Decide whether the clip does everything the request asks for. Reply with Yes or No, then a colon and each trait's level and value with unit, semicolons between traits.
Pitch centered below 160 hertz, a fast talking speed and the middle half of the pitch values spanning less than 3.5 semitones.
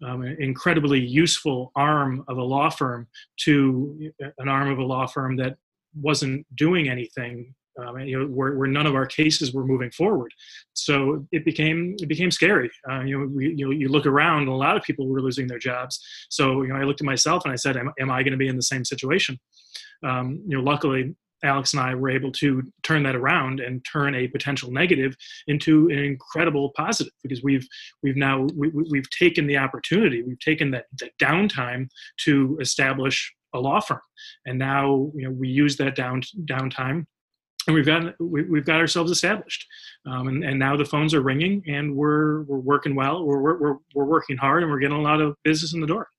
Yes: medium, 140 Hz; fast, 210 wpm; narrow, 2.6 semitones